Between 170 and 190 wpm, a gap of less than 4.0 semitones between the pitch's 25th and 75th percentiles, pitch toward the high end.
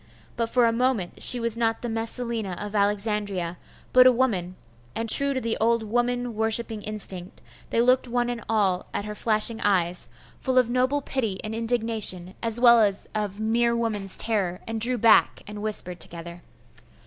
Yes: average, 175 wpm; average, 2.8 semitones; high, 225 Hz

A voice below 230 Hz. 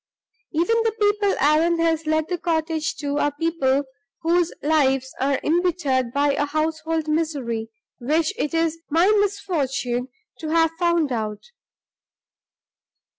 No: very high, 315 Hz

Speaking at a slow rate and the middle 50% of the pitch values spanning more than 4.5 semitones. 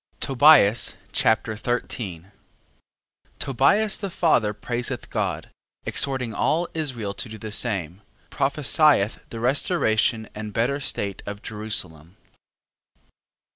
Yes: slow, 100 wpm; average, 4.9 semitones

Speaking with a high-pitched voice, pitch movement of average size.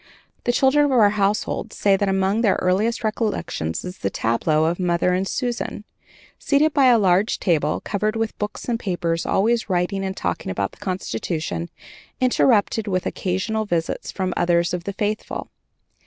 Yes: high, 195 Hz; average, 4.0 semitones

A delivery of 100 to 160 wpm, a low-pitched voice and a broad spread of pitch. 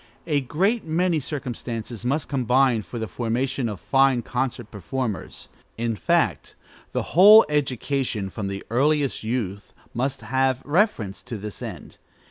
No: slow, 135 wpm; low, 130 Hz; average, 3.9 semitones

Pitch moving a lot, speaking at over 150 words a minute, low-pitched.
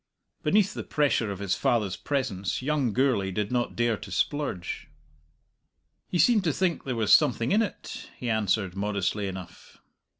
Yes: wide, 6.4 semitones; average, 160 wpm; low, 115 Hz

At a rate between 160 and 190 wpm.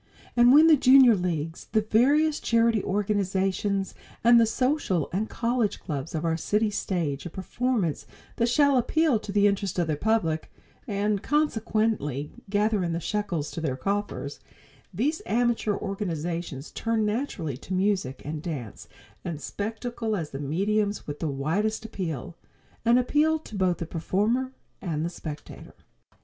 No: average, 150 wpm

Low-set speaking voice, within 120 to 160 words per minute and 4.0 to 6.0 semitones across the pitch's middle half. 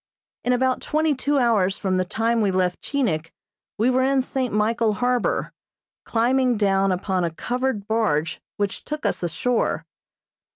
No: high, 225 Hz; average, 155 wpm; average, 4.8 semitones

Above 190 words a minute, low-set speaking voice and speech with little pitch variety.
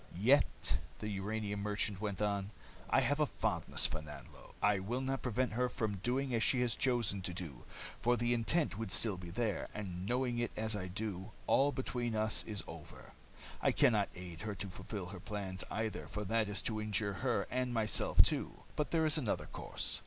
No: average, 200 wpm; low, 110 Hz; average, 3.6 semitones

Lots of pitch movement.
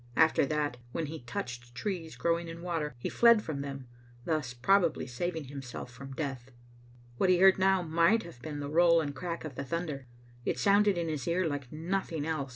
No: average, 4.0 semitones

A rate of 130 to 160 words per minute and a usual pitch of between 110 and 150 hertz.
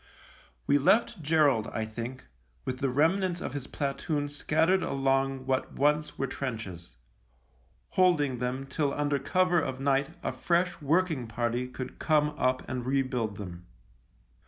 Yes: average, 140 wpm; low, 135 Hz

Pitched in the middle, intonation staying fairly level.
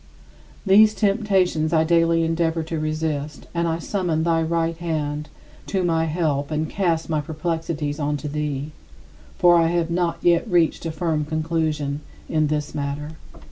Yes: medium, 160 Hz; narrow, 1.9 semitones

